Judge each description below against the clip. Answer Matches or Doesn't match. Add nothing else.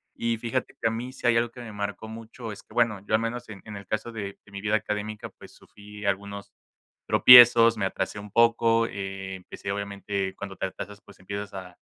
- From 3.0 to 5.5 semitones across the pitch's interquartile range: Doesn't match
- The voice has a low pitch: Matches